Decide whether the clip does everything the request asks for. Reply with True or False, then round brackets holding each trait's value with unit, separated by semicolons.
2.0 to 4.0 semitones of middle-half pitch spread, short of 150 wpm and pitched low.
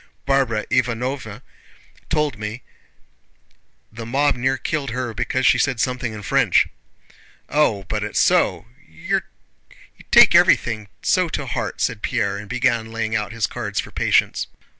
True (3.3 semitones; 140 wpm; 120 Hz)